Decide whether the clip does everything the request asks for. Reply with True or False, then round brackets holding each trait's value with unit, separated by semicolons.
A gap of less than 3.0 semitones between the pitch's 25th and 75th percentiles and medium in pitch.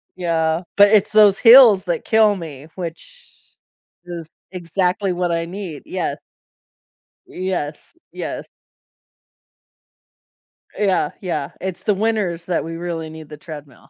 False (3.7 semitones; 175 Hz)